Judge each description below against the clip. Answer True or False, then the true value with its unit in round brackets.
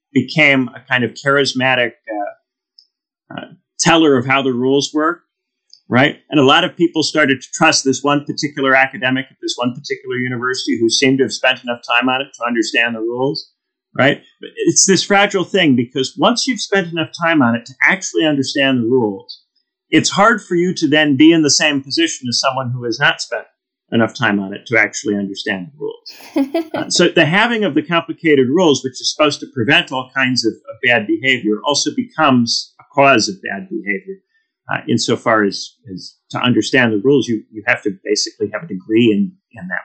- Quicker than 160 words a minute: True (200 wpm)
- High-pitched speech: False (140 Hz)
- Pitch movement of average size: False (6.4 semitones)